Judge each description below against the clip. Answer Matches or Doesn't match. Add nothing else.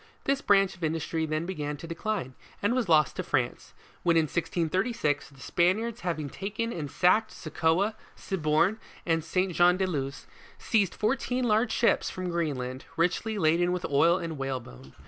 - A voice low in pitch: Doesn't match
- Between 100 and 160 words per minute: Doesn't match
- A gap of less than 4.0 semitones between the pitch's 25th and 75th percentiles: Doesn't match